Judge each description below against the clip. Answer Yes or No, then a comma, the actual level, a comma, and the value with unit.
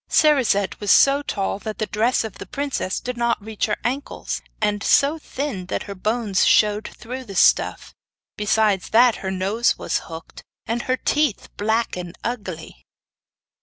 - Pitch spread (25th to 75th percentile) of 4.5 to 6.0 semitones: No, average, 3.8 semitones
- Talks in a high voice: Yes, high, 220 Hz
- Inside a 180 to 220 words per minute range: No, average, 165 wpm